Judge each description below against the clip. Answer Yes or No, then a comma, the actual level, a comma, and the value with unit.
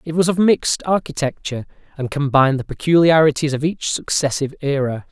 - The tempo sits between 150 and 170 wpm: Yes, average, 155 wpm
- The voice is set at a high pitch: No, medium, 150 Hz